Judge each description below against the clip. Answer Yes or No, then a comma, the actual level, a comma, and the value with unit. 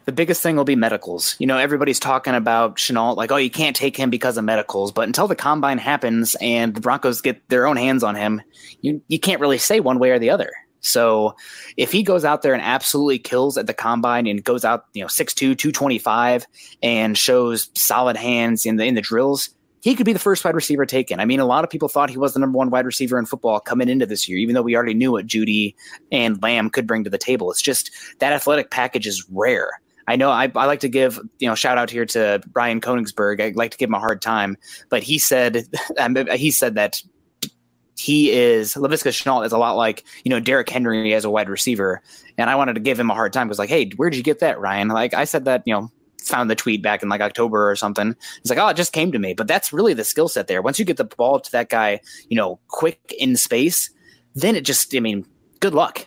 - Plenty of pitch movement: No, average, 4.2 semitones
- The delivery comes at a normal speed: No, fast, 255 wpm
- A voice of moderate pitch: No, low, 125 Hz